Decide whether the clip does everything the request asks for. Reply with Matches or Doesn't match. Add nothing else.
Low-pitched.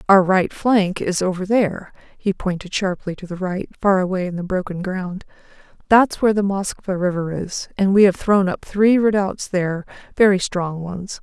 Doesn't match